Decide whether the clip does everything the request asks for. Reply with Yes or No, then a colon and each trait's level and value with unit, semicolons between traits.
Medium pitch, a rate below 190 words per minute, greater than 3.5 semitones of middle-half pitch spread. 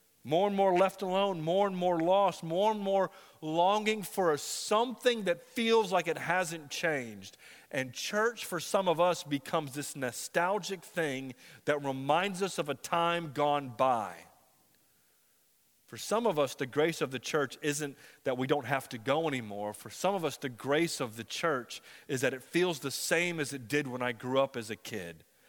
No: medium, 160 Hz; average, 195 wpm; wide, 5.6 semitones